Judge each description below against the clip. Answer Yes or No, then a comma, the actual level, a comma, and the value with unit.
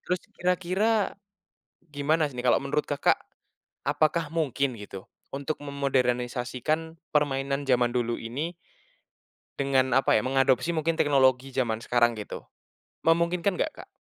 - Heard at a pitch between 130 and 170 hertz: Yes, medium, 140 Hz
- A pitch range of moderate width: Yes, average, 4.1 semitones